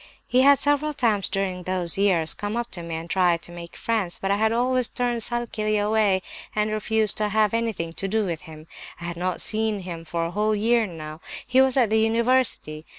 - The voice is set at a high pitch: Yes, high, 210 Hz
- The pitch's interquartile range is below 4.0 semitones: No, average, 4.8 semitones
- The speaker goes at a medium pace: No, fast, 215 wpm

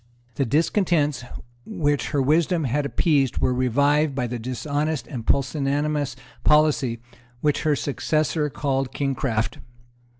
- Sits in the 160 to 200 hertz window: No, medium, 145 Hz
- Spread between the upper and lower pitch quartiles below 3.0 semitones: Yes, narrow, 2.6 semitones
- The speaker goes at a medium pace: No, slow, 120 wpm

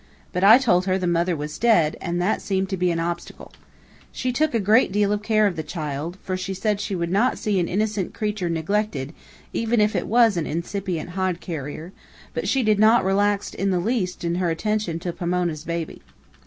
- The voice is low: No, medium, 185 Hz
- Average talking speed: No, fast, 210 wpm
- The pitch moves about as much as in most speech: Yes, average, 3.7 semitones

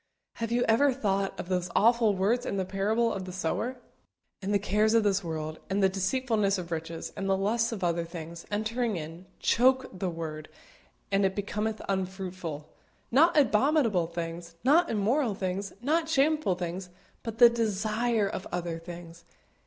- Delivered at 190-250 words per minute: No, average, 170 wpm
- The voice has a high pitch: Yes, high, 195 Hz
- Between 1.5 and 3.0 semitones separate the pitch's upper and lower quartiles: No, average, 4.5 semitones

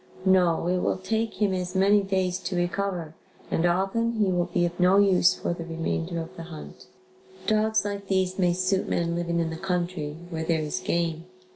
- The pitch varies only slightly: Yes, narrow, 2.2 semitones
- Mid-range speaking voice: Yes, medium, 180 Hz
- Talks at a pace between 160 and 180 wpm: No, average, 195 wpm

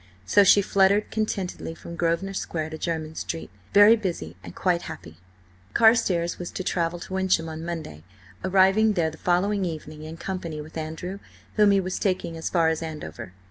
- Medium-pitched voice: Yes, medium, 175 Hz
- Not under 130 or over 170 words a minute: No, average, 180 wpm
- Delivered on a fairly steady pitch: No, average, 3.2 semitones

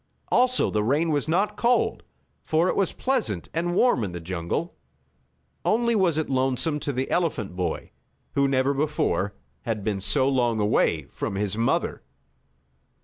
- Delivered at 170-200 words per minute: No, average, 155 wpm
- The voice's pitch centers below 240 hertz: Yes, medium, 140 Hz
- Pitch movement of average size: No, wide, 8.4 semitones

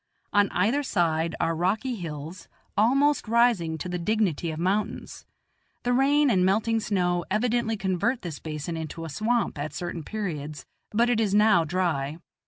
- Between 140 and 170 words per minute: Yes, average, 160 wpm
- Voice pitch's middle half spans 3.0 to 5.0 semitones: No, wide, 5.4 semitones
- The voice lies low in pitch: No, medium, 185 Hz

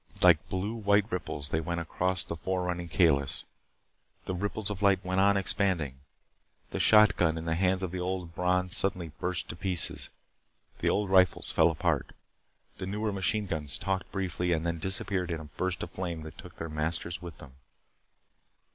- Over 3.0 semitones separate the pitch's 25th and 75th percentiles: No, narrow, 2.5 semitones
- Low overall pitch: Yes, very low, 90 Hz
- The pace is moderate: Yes, average, 180 wpm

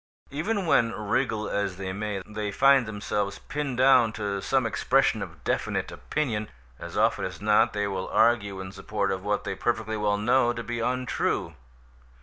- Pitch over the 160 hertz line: No, low, 105 Hz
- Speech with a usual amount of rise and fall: Yes, average, 3.3 semitones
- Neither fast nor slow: Yes, average, 170 wpm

